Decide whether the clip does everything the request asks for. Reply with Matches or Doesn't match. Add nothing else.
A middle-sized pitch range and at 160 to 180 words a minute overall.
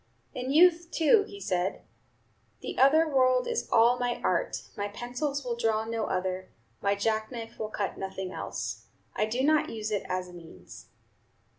Matches